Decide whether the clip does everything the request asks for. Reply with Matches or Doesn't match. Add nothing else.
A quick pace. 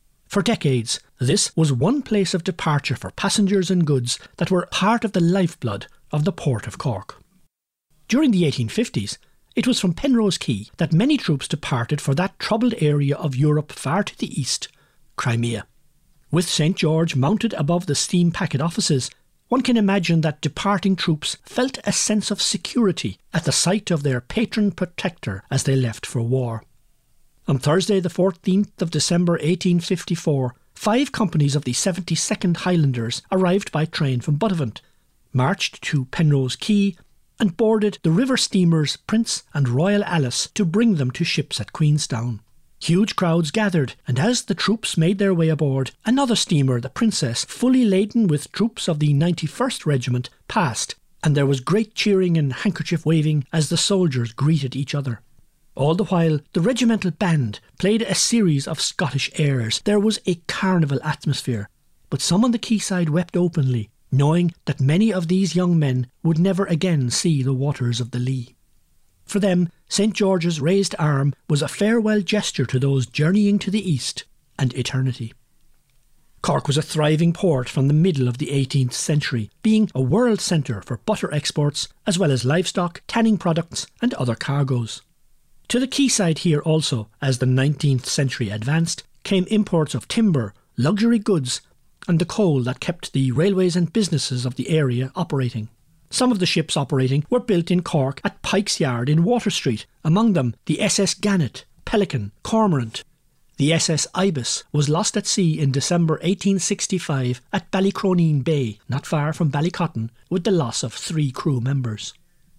Doesn't match